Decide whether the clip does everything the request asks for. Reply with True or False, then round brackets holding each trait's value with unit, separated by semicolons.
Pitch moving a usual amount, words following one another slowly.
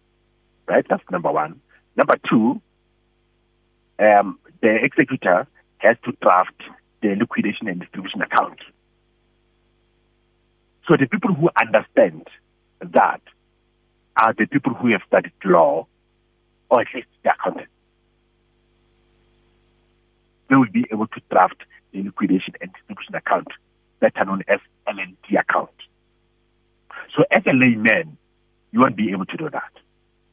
True (4.6 semitones; 125 wpm)